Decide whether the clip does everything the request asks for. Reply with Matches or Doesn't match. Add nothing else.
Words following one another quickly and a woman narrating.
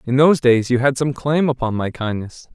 Doesn't match